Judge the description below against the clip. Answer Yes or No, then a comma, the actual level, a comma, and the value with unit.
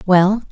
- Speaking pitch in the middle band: No, high, 195 Hz